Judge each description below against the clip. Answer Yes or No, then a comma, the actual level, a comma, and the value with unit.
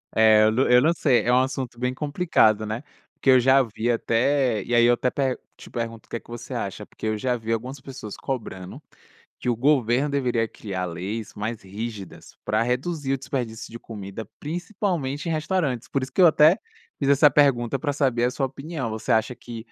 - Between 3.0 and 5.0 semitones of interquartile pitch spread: Yes, average, 3.7 semitones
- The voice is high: No, low, 125 Hz